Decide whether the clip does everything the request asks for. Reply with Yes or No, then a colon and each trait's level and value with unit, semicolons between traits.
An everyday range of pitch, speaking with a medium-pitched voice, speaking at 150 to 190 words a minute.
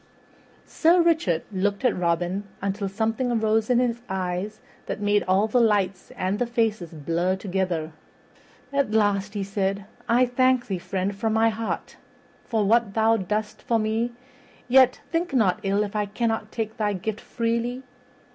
No: average, 3.1 semitones; high, 215 Hz; average, 160 wpm